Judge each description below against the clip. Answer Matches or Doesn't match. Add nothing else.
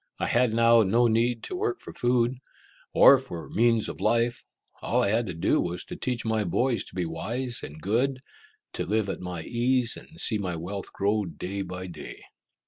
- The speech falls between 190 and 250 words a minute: Matches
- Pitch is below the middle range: Matches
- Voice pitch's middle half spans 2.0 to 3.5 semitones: Doesn't match